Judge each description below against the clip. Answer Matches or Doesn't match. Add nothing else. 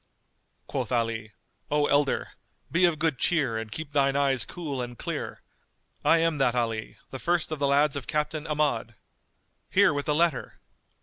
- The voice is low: Doesn't match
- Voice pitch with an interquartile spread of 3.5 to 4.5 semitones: Matches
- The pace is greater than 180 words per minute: Doesn't match